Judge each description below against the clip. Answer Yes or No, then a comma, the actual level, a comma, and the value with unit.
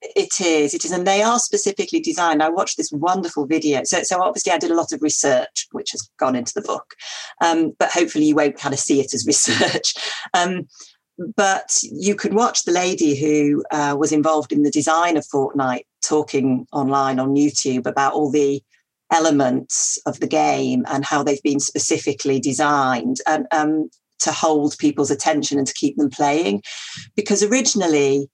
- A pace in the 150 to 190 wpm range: Yes, average, 180 wpm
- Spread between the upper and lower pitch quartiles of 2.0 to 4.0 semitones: Yes, average, 3.7 semitones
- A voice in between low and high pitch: Yes, medium, 150 Hz